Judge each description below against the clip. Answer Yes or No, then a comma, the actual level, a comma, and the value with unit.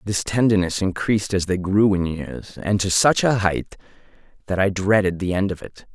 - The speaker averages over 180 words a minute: Yes, average, 200 wpm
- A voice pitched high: No, very low, 95 Hz